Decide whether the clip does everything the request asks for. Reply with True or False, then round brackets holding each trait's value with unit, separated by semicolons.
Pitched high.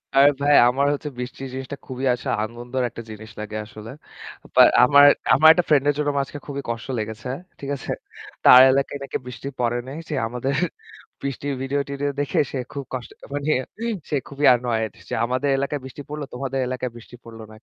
False (135 Hz)